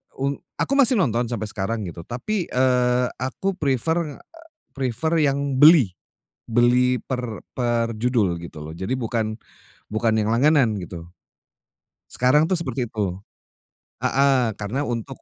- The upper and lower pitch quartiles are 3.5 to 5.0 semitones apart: Yes, average, 4.0 semitones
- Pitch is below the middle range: Yes, low, 125 Hz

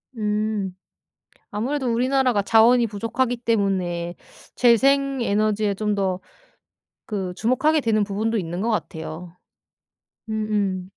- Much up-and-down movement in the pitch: No, average, 3.3 semitones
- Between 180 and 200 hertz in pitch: No, high, 215 Hz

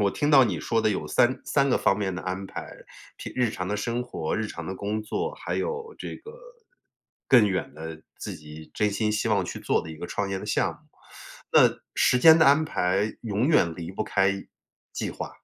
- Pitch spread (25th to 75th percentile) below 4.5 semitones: No, average, 5.1 semitones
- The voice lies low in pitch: Yes, low, 105 Hz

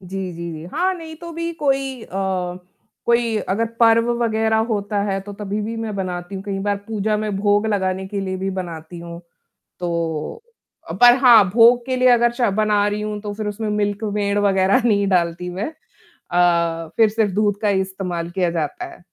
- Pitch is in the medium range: No, high, 205 Hz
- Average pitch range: Yes, average, 3.2 semitones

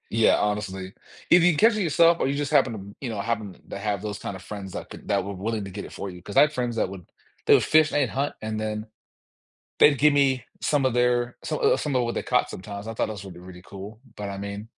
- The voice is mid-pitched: No, low, 110 Hz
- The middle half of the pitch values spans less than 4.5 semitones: No, wide, 5.4 semitones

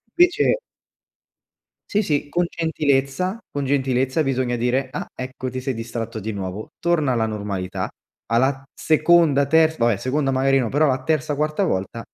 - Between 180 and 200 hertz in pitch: No, low, 135 Hz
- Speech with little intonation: No, average, 4.2 semitones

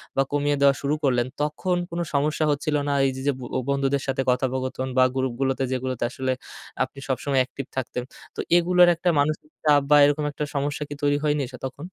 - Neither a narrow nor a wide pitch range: No, narrow, 2.1 semitones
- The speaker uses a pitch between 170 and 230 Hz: No, medium, 140 Hz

